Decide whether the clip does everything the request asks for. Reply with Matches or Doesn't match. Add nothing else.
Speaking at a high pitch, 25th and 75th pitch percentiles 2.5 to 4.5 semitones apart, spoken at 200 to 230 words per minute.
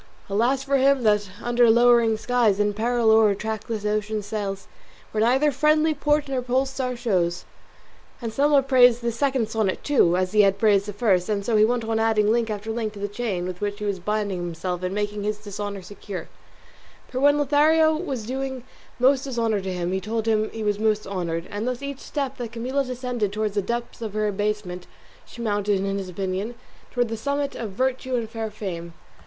Matches